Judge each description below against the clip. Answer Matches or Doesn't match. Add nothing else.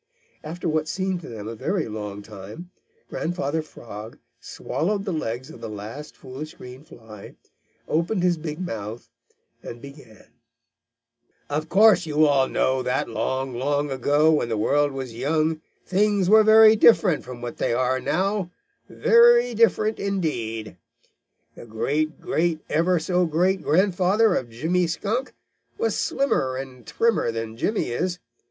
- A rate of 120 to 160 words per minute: Matches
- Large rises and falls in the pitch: Matches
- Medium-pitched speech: Matches